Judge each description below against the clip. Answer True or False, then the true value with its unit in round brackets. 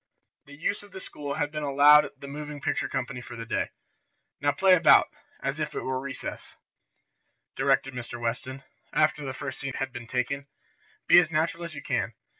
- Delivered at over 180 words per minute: True (190 wpm)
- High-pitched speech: False (140 Hz)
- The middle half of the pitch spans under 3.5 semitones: True (2.4 semitones)